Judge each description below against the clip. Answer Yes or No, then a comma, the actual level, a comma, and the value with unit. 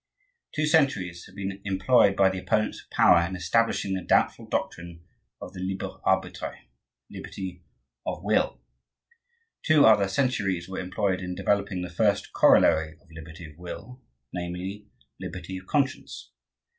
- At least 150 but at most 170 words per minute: No, average, 140 wpm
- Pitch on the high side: No, very low, 95 Hz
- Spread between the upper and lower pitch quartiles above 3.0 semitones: No, narrow, 2.4 semitones